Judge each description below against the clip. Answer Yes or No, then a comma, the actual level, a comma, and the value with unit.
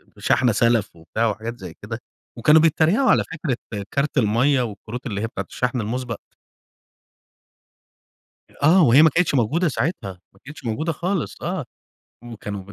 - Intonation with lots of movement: Yes, wide, 5.8 semitones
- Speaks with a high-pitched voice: No, low, 120 Hz